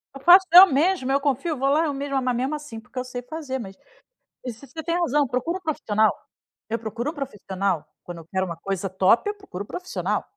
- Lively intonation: Yes, wide, 5.9 semitones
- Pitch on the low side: No, very high, 265 Hz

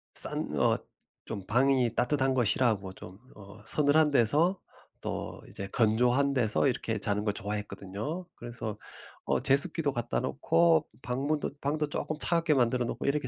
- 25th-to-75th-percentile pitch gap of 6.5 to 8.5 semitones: No, average, 5.1 semitones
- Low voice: Yes, low, 125 Hz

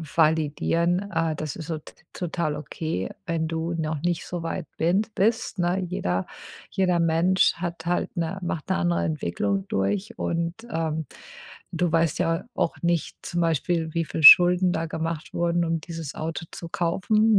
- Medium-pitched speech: Yes, medium, 165 Hz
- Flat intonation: Yes, narrow, 1.7 semitones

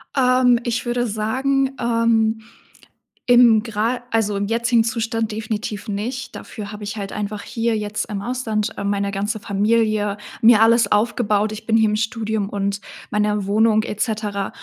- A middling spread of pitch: No, narrow, 1.9 semitones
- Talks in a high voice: Yes, high, 220 Hz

